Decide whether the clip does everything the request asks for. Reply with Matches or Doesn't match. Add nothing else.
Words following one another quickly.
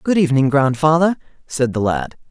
Doesn't match